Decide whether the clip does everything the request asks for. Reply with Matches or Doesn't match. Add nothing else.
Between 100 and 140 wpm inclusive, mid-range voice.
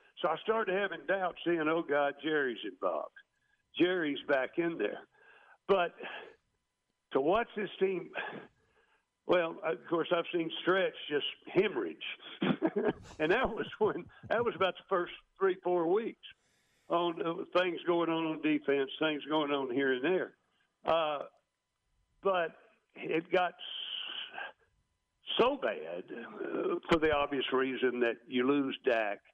Matches